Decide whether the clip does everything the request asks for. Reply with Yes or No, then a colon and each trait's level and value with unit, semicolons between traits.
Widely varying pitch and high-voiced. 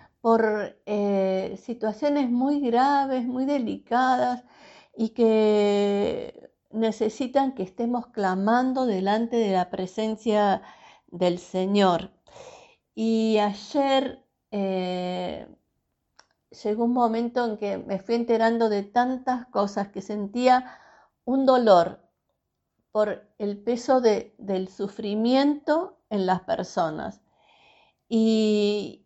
No: average, 3.9 semitones; high, 220 Hz